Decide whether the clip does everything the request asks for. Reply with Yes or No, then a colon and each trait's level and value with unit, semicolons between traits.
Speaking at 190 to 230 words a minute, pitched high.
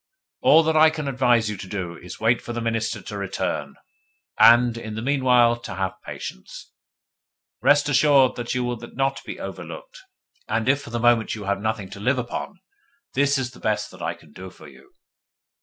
No: average, 200 wpm; low, 120 Hz